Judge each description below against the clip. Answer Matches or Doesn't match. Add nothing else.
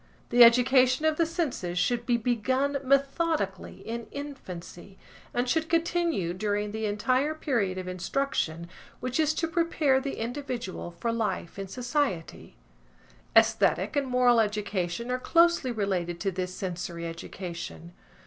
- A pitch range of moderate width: Doesn't match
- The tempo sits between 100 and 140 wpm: Matches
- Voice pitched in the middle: Doesn't match